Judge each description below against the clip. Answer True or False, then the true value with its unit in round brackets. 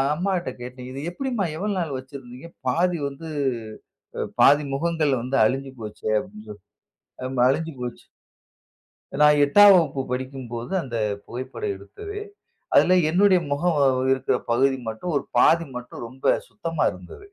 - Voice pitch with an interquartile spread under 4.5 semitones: False (5.4 semitones)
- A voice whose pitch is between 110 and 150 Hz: True (140 Hz)